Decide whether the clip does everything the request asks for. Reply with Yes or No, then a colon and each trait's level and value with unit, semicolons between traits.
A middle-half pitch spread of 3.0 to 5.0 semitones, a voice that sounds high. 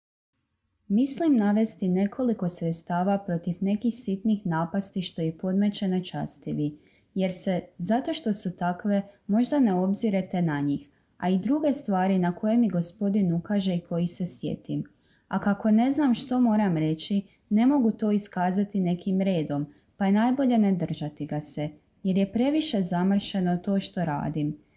Yes: average, 3.6 semitones; high, 195 Hz